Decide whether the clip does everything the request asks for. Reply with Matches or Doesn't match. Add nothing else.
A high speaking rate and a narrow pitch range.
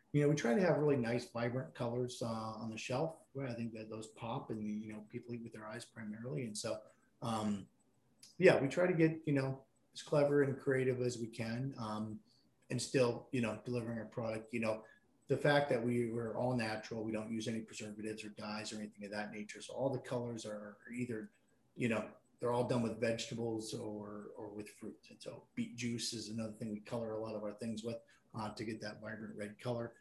Matches